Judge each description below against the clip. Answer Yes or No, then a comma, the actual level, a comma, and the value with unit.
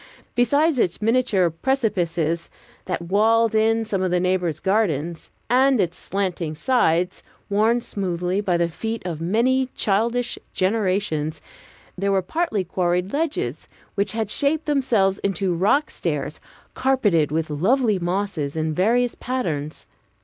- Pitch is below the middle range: No, high, 195 Hz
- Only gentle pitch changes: No, average, 5.0 semitones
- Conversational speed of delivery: No, slow, 130 wpm